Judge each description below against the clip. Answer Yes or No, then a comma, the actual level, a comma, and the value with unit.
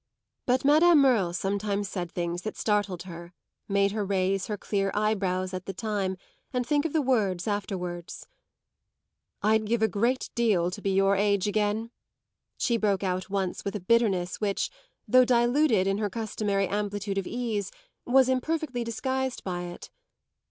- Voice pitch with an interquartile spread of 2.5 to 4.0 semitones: Yes, average, 3.6 semitones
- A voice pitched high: Yes, high, 205 Hz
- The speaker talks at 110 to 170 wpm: Yes, average, 160 wpm